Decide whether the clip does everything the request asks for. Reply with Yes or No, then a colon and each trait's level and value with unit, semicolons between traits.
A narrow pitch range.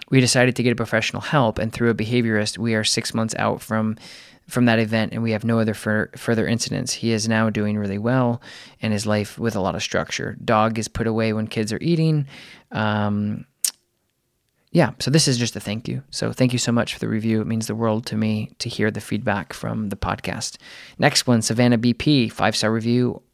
Yes: narrow, 2.0 semitones